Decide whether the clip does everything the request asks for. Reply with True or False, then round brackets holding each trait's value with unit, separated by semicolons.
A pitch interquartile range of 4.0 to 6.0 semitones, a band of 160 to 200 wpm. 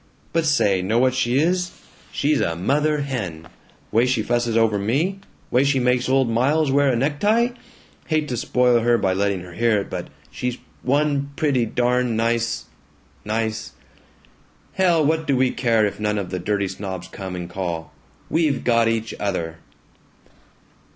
True (5.4 semitones; 165 wpm)